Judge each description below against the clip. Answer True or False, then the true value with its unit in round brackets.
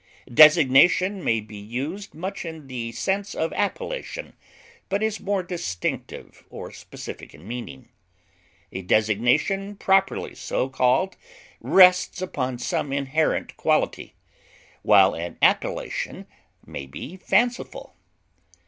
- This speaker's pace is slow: True (110 wpm)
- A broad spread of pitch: True (8.6 semitones)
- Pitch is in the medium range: True (155 Hz)